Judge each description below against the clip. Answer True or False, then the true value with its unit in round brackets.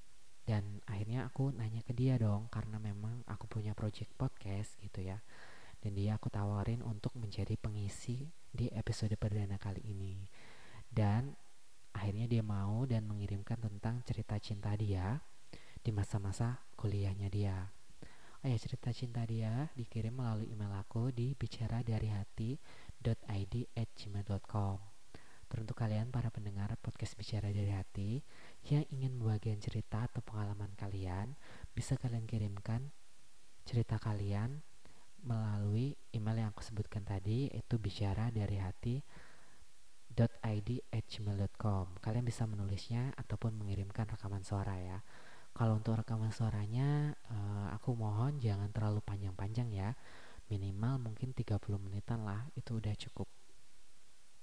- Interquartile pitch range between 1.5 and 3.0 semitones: True (2.6 semitones)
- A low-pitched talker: True (110 Hz)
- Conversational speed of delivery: True (120 wpm)